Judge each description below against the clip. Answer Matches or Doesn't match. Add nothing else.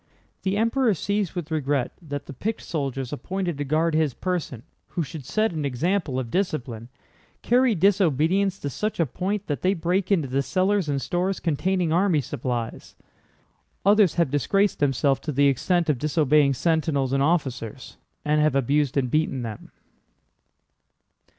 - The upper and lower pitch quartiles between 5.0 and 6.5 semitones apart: Matches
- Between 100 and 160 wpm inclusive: Matches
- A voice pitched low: Doesn't match